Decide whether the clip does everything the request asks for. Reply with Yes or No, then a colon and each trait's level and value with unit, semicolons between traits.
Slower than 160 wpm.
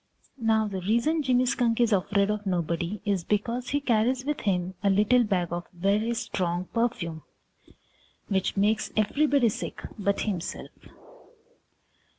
Yes: average, 140 wpm